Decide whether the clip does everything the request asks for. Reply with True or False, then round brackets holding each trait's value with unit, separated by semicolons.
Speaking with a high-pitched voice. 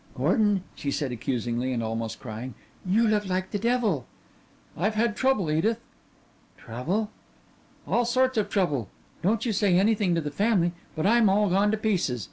True (195 Hz)